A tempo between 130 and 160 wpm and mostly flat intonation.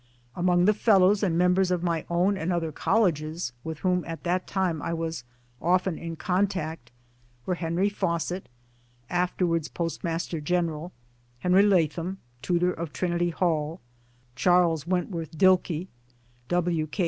Yes: slow, 135 wpm; narrow, 1.9 semitones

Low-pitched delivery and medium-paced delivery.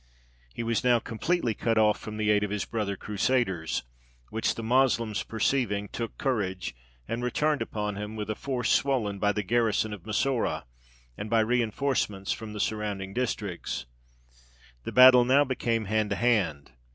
Yes: low, 110 Hz; average, 165 wpm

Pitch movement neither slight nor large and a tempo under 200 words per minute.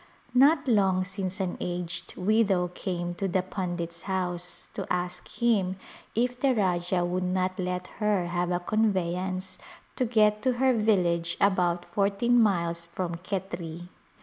Yes: average, 3.1 semitones; average, 145 wpm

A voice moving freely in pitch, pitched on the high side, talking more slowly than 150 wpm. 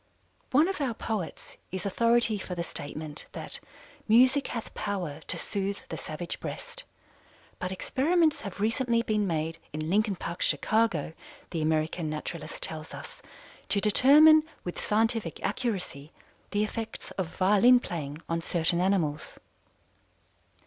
Yes: wide, 5.7 semitones; high, 200 Hz; slow, 135 wpm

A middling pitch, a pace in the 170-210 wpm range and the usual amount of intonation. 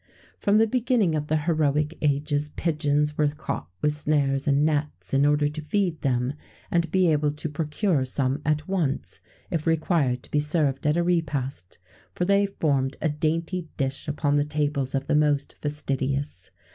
No: medium, 150 Hz; average, 175 wpm; narrow, 2.3 semitones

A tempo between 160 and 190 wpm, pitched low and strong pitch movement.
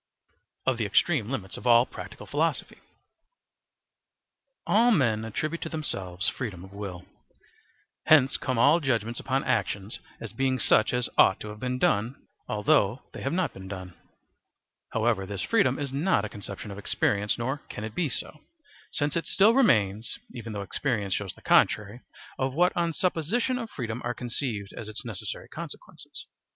Yes: average, 165 wpm; low, 120 Hz; wide, 5.9 semitones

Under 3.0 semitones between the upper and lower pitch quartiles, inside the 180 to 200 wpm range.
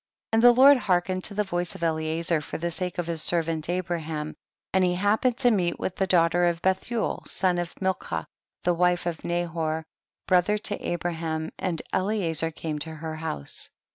Yes: narrow, 2.6 semitones; average, 195 wpm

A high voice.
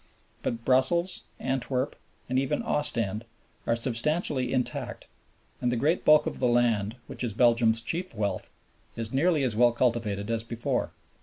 No: low, 120 Hz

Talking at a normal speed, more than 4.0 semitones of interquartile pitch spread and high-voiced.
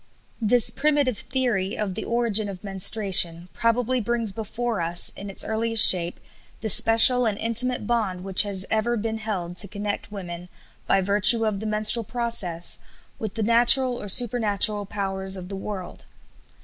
No: average, 160 wpm; average, 3.2 semitones; high, 210 Hz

